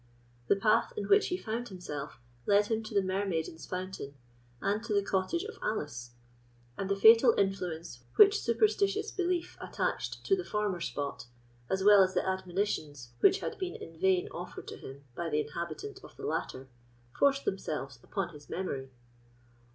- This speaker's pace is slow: No, average, 165 wpm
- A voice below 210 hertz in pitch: Yes, high, 190 Hz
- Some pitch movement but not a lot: No, wide, 6.1 semitones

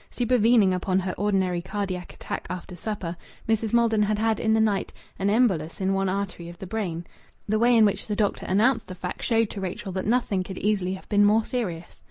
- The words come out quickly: Yes, fast, 215 wpm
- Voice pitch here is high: Yes, high, 200 Hz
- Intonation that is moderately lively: Yes, average, 3.0 semitones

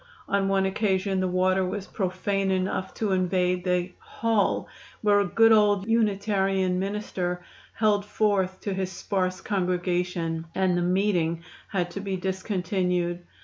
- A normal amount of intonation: No, narrow, 1.8 semitones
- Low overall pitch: No, high, 190 Hz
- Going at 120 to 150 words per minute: Yes, average, 140 wpm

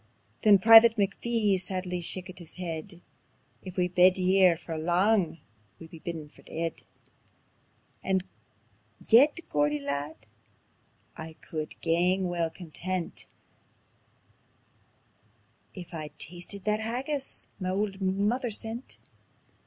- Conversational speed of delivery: No, slow, 110 wpm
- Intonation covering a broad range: No, average, 3.6 semitones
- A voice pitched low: No, medium, 185 Hz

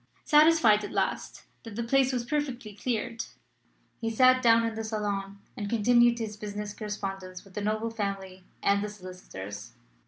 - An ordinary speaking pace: Yes, average, 160 wpm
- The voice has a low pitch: No, high, 215 Hz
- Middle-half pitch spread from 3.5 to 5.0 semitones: No, average, 2.9 semitones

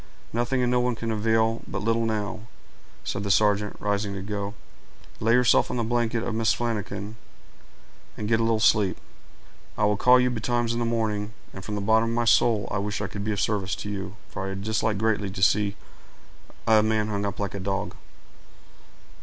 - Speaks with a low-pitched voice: Yes, low, 110 Hz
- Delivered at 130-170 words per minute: No, fast, 205 wpm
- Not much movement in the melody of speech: Yes, narrow, 2.1 semitones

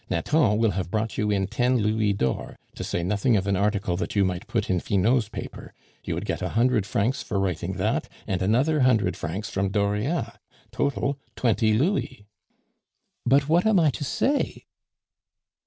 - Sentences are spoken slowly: No, average, 175 wpm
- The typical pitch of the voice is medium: No, low, 105 Hz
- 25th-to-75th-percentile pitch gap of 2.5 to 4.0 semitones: No, average, 4.8 semitones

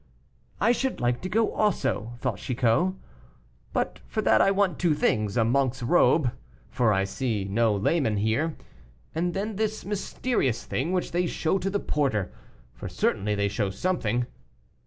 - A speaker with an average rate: Yes, average, 160 wpm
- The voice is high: No, low, 135 Hz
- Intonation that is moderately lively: No, wide, 8.9 semitones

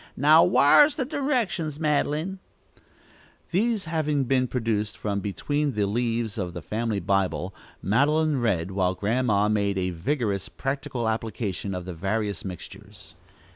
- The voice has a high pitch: No, low, 115 Hz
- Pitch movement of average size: No, wide, 7.0 semitones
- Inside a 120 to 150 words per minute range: Yes, slow, 135 wpm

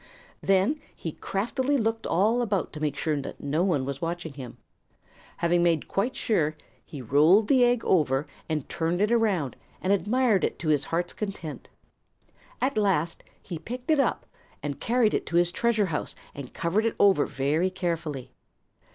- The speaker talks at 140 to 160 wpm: No, average, 170 wpm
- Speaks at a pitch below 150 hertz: No, medium, 175 Hz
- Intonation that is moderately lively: No, wide, 6.0 semitones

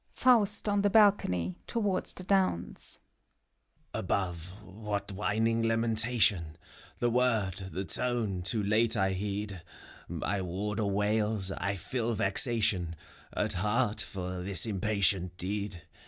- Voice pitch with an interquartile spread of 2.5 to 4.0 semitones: Yes, average, 3.4 semitones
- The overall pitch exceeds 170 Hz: No, low, 105 Hz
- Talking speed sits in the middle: No, slow, 120 wpm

